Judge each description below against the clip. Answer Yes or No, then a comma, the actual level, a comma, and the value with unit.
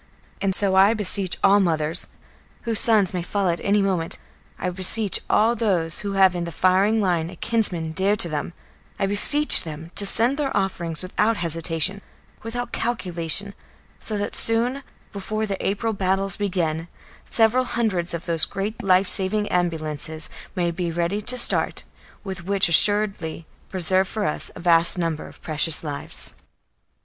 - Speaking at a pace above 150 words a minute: Yes, average, 160 wpm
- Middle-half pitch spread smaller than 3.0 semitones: No, average, 3.5 semitones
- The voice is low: No, high, 190 Hz